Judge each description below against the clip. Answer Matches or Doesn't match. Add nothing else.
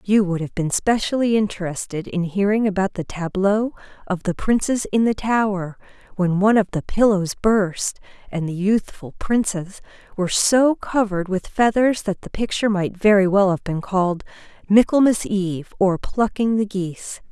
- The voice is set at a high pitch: Matches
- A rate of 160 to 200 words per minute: Matches